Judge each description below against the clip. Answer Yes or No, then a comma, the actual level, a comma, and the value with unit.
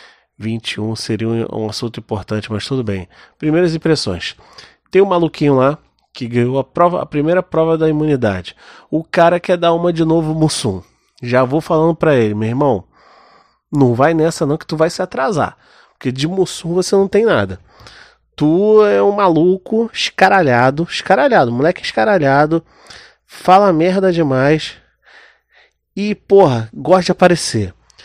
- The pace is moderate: Yes, average, 150 wpm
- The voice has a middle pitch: Yes, medium, 155 Hz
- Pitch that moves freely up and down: Yes, wide, 6.9 semitones